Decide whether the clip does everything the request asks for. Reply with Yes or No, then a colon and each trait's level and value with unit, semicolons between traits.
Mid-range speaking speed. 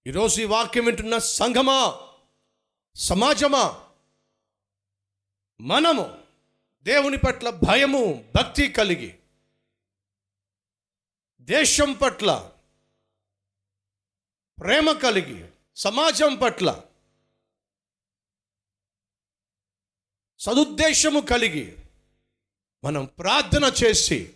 No: slow, 60 wpm